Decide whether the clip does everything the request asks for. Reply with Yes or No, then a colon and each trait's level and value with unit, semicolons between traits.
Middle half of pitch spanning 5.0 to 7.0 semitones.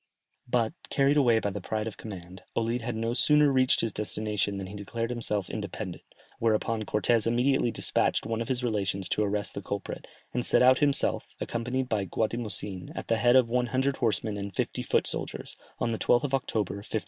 No: average, 3.1 semitones